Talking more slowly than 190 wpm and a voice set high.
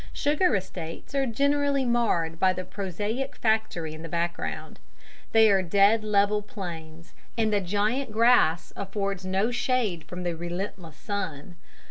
Yes: average, 140 wpm; high, 200 Hz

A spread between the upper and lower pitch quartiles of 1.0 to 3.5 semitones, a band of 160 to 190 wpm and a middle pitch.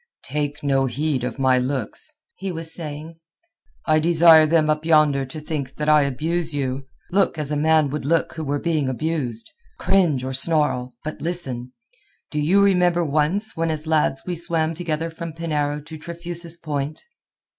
Yes: average, 2.7 semitones; average, 165 wpm; medium, 155 Hz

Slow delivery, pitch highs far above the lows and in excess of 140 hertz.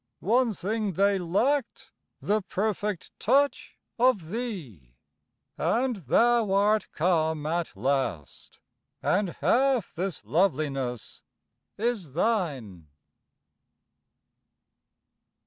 Yes: slow, 80 wpm; wide, 6.7 semitones; high, 190 Hz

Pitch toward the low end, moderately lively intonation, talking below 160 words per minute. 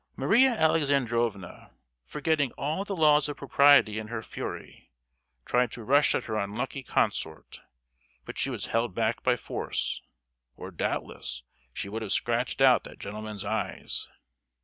Yes: low, 120 Hz; average, 5.0 semitones; average, 145 wpm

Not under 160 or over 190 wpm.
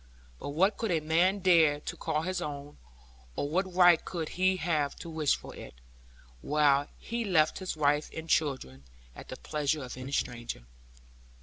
Yes: average, 175 wpm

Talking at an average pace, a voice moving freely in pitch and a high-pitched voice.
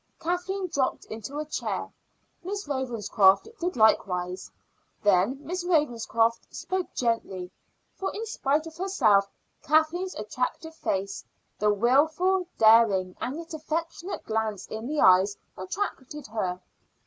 No: slow, 120 wpm; wide, 8.1 semitones; very high, 260 Hz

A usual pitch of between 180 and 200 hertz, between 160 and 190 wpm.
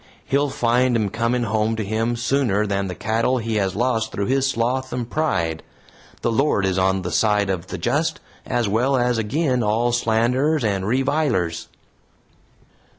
No: low, 115 Hz; average, 165 wpm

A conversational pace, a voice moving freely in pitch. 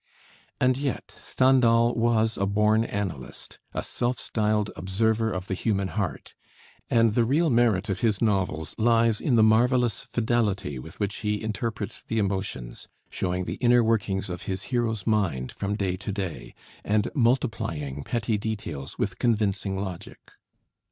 No: average, 150 wpm; average, 3.3 semitones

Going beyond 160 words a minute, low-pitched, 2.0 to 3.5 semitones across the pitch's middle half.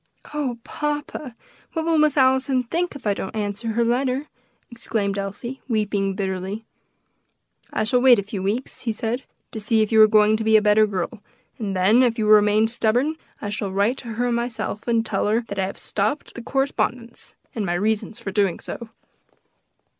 No: average, 190 wpm; high, 220 Hz; average, 3.2 semitones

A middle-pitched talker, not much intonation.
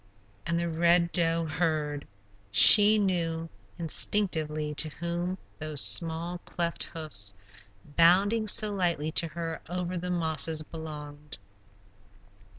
Yes: medium, 165 Hz; narrow, 2.3 semitones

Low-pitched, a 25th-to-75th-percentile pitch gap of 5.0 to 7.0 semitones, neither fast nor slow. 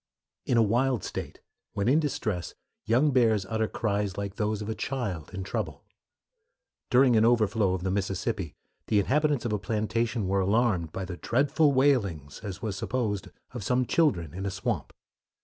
No: low, 110 Hz; average, 4.1 semitones; average, 170 wpm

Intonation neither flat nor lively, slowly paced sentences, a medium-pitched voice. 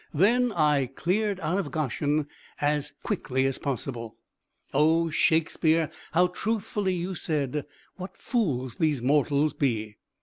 Yes: average, 4.6 semitones; slow, 125 wpm; medium, 155 Hz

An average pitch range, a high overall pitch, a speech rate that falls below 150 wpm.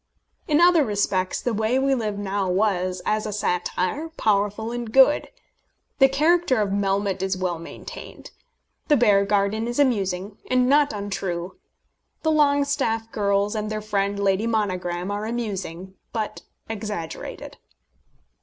Yes: average, 3.7 semitones; high, 210 Hz; slow, 135 wpm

